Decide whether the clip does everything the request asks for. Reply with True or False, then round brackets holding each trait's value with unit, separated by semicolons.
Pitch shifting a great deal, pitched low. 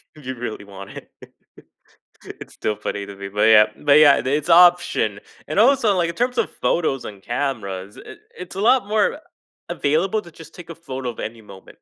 False (8.8 semitones; 145 Hz)